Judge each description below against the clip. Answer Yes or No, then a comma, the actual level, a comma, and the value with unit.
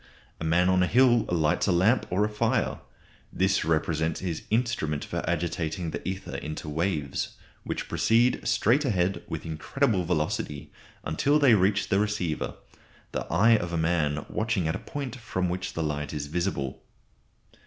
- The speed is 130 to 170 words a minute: Yes, average, 165 wpm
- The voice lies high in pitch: No, very low, 90 Hz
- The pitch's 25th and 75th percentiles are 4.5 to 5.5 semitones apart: Yes, average, 5.1 semitones